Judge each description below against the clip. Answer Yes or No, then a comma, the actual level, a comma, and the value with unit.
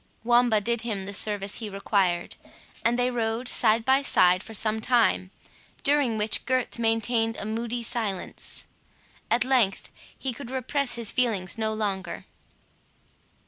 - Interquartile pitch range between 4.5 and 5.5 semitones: No, average, 2.7 semitones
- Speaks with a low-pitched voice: No, high, 225 Hz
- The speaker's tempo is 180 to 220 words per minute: No, average, 140 wpm